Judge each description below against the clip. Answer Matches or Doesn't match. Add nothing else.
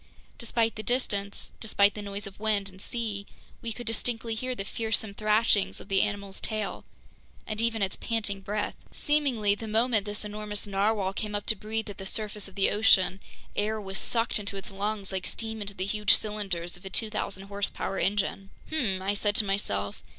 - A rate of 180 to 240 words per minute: Matches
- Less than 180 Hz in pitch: Doesn't match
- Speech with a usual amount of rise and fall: Doesn't match